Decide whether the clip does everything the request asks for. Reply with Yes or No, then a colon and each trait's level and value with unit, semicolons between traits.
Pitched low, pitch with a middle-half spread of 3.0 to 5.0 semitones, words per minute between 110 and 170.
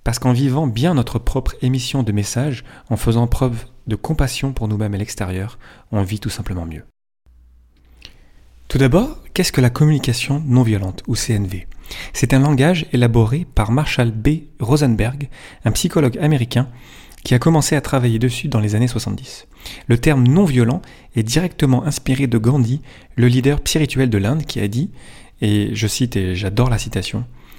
Yes: low, 125 Hz; average, 4.2 semitones; average, 165 wpm